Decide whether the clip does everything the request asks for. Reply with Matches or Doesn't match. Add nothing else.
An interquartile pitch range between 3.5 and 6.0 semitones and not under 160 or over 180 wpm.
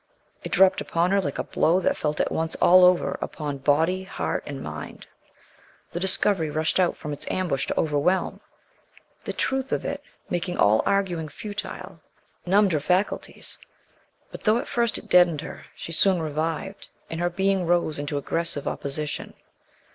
Matches